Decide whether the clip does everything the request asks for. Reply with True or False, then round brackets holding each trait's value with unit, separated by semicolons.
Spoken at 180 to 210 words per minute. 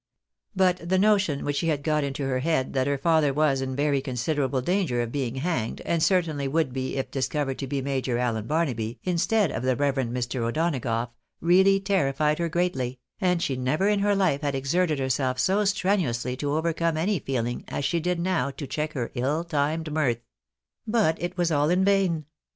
True (195 wpm)